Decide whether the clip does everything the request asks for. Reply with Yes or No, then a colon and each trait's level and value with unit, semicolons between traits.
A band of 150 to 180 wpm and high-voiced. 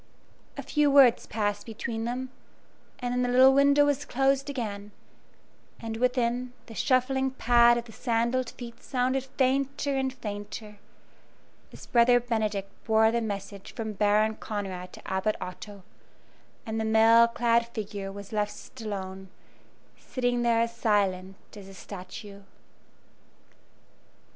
No: slow, 135 wpm; high, 230 Hz